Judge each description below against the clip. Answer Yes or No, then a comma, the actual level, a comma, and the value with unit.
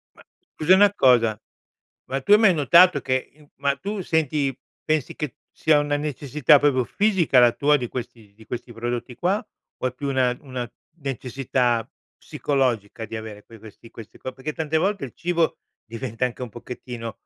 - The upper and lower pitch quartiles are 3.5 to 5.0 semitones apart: Yes, average, 4.2 semitones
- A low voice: Yes, low, 130 Hz